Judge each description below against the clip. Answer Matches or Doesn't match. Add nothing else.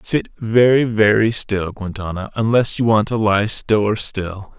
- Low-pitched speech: Matches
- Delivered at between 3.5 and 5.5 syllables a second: Matches